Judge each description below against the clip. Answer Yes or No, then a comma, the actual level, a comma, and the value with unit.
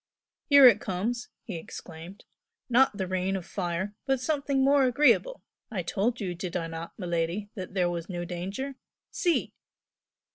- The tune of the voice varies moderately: No, wide, 6.4 semitones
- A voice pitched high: Yes, high, 195 Hz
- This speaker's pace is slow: No, average, 155 wpm